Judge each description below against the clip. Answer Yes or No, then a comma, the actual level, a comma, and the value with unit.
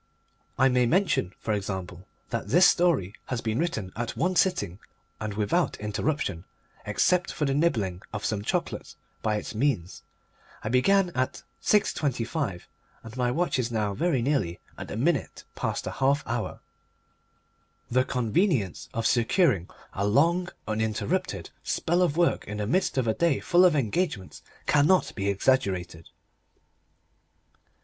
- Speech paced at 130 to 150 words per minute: Yes, average, 145 wpm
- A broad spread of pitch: Yes, wide, 7.6 semitones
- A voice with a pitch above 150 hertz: No, low, 125 Hz